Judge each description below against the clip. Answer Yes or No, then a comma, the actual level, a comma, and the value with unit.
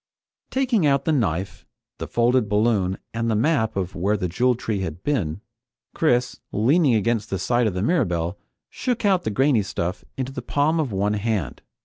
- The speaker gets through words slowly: No, average, 180 wpm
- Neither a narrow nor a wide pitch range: No, wide, 6.0 semitones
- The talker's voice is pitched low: Yes, low, 115 Hz